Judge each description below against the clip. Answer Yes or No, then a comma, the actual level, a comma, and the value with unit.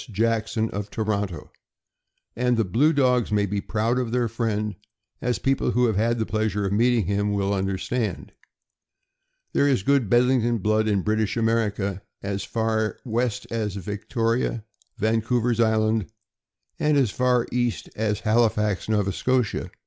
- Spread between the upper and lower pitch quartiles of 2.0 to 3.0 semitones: Yes, narrow, 2.6 semitones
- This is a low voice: Yes, low, 110 Hz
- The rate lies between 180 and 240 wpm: No, average, 145 wpm